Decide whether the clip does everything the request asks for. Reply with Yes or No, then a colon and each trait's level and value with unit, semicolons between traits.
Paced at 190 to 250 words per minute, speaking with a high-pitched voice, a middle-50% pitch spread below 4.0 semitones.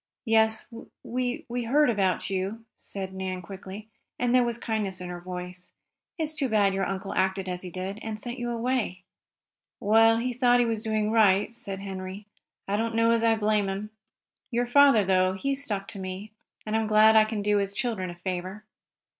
Yes: average, 195 wpm; high, 215 Hz; average, 3.3 semitones